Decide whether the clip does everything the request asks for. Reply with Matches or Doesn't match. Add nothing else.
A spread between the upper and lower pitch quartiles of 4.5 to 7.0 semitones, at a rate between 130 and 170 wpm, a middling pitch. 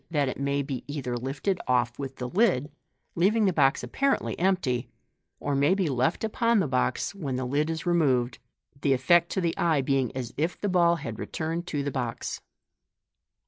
Doesn't match